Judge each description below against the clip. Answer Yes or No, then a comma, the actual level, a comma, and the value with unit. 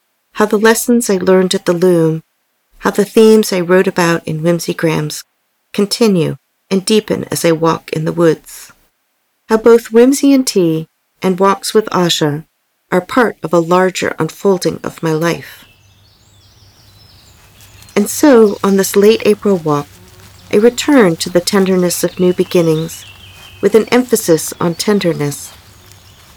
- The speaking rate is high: No, average, 145 wpm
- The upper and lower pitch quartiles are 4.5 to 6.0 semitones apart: Yes, average, 5.2 semitones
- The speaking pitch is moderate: Yes, medium, 175 Hz